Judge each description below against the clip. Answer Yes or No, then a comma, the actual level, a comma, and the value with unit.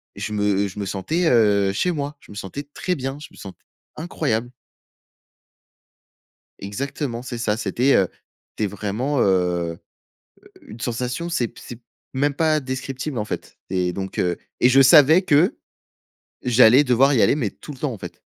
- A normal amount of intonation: No, wide, 5.8 semitones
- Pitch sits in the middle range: No, low, 120 Hz